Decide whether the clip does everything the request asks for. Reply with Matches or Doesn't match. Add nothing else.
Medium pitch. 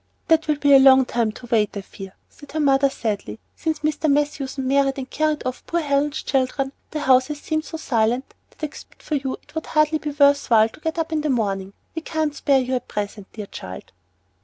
Doesn't match